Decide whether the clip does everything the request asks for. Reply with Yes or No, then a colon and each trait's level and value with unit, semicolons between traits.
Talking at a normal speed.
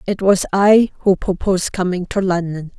Yes: average, 170 wpm